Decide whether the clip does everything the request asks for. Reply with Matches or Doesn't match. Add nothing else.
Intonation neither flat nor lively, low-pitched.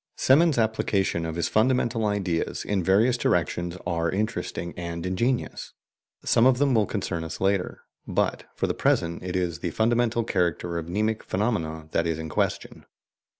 Matches